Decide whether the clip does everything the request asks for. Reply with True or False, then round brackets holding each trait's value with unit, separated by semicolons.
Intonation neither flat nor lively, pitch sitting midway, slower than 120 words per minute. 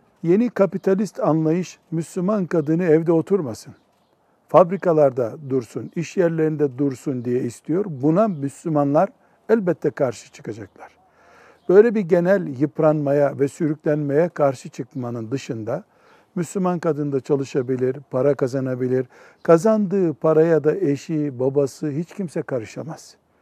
True (4.0 semitones; 155 Hz; 110 wpm)